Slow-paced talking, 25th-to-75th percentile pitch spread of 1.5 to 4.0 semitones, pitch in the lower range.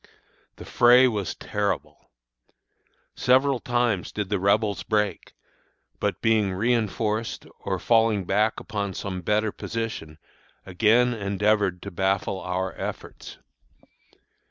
Yes: slow, 110 wpm; average, 2.8 semitones; low, 105 Hz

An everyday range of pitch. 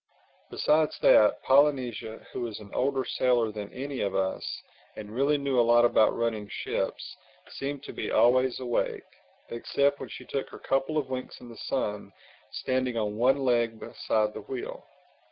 Yes: average, 3.6 semitones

